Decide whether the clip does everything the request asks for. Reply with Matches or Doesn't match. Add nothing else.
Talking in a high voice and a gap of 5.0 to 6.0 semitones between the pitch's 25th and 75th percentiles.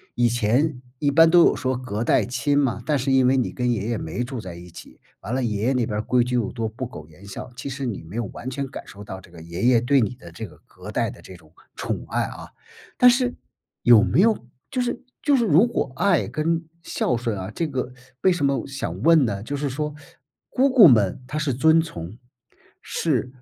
Doesn't match